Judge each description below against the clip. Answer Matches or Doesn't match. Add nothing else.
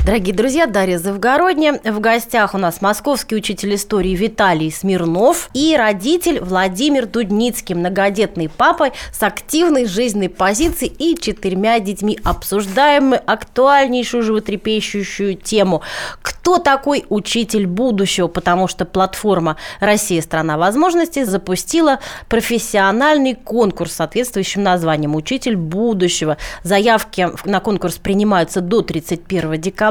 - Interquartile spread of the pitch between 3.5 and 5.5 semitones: Matches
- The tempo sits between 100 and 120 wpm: Matches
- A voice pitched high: Matches